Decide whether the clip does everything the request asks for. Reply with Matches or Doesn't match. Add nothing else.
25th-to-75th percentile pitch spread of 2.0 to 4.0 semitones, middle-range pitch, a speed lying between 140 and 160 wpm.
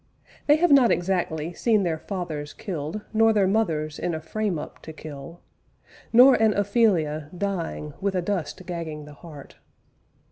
Doesn't match